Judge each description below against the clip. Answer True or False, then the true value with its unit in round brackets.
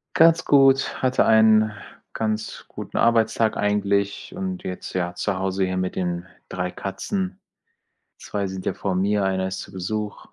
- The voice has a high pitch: False (105 Hz)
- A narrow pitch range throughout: False (3.1 semitones)